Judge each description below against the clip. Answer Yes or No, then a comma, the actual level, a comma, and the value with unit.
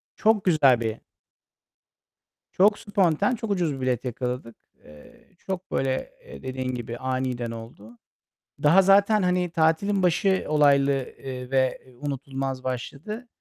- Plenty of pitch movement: Yes, wide, 6.4 semitones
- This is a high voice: No, medium, 140 Hz